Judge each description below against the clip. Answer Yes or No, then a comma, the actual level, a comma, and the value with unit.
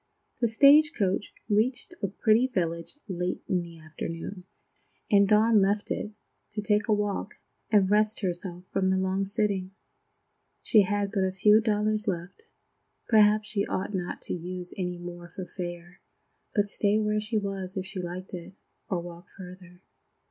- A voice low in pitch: No, high, 195 Hz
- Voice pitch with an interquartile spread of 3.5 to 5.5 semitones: No, average, 2.8 semitones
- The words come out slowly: No, average, 165 wpm